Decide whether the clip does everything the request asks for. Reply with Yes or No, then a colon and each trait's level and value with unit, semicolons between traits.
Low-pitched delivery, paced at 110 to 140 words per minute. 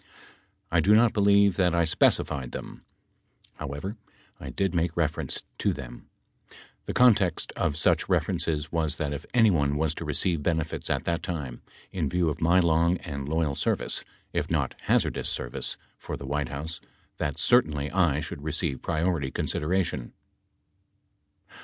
No: very low, 80 Hz; average, 150 wpm